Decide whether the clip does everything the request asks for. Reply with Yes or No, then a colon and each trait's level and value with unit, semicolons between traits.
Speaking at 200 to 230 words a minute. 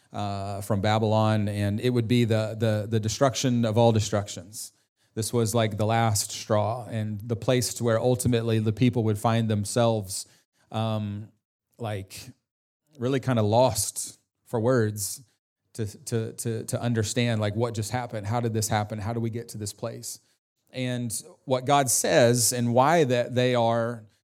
No: average, 170 wpm